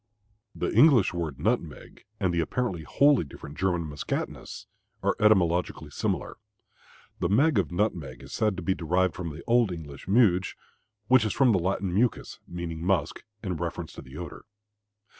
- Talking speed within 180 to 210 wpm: No, average, 160 wpm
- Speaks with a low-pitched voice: Yes, very low, 90 Hz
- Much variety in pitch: No, average, 4.3 semitones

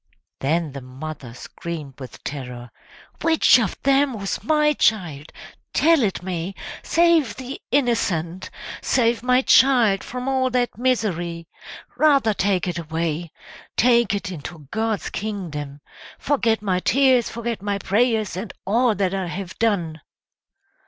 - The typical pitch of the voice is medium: No, high, 200 Hz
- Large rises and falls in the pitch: Yes, wide, 6.8 semitones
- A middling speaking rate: No, slow, 130 wpm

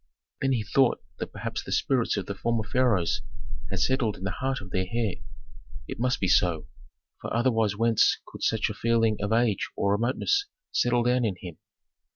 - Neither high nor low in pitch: No, low, 115 Hz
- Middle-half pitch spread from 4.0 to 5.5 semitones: No, average, 3.5 semitones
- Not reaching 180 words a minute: No, average, 190 wpm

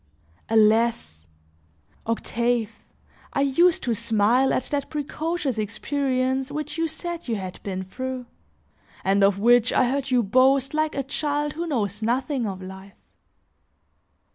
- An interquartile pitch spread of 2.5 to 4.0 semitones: No, average, 4.8 semitones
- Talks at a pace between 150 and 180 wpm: No, slow, 135 wpm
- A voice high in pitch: Yes, very high, 255 Hz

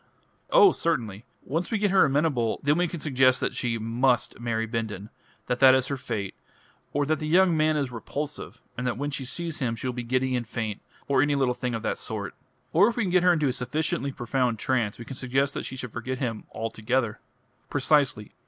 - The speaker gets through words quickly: Yes, fast, 225 wpm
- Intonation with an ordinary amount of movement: Yes, average, 4.2 semitones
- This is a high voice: No, low, 130 Hz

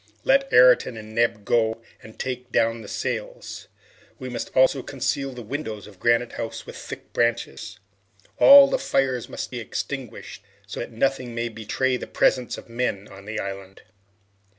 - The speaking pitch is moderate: No, low, 120 Hz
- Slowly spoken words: No, average, 165 wpm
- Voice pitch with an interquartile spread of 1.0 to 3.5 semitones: Yes, average, 2.8 semitones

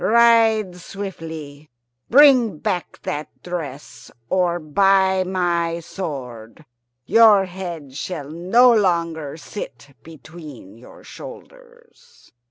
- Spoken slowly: Yes, slow, 90 wpm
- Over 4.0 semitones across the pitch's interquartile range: Yes, average, 4.9 semitones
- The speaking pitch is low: No, medium, 175 Hz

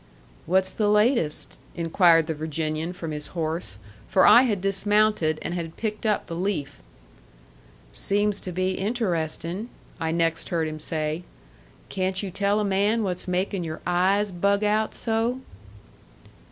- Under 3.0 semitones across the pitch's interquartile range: No, average, 4.0 semitones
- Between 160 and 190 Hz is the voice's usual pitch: Yes, medium, 185 Hz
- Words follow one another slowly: No, average, 145 wpm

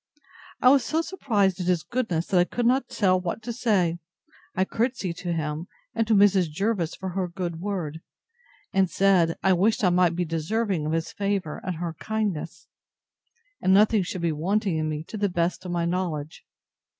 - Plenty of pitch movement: No, average, 3.6 semitones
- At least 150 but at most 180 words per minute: No, average, 190 wpm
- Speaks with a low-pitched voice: No, medium, 185 Hz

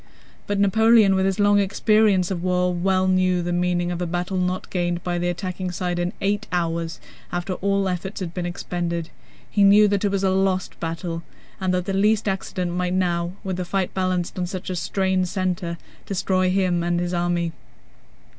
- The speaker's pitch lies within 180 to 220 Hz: Yes, medium, 185 Hz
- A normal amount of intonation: No, narrow, 1.7 semitones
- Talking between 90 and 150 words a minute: No, average, 185 wpm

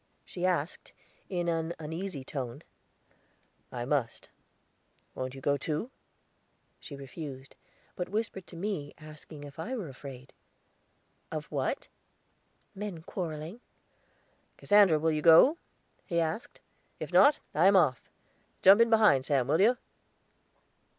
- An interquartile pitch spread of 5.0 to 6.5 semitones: Yes, average, 5.3 semitones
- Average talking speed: No, slow, 125 wpm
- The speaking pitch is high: No, medium, 160 Hz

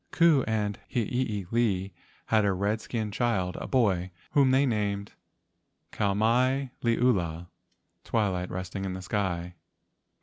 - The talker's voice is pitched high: No, low, 105 Hz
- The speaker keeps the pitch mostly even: No, average, 4.3 semitones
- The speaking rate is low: Yes, slow, 125 wpm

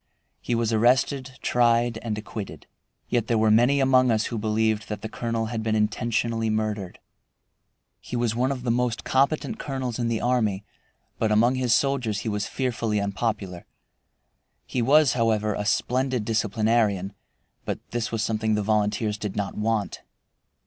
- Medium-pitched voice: No, low, 115 Hz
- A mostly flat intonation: Yes, narrow, 2.3 semitones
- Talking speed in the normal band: Yes, average, 160 wpm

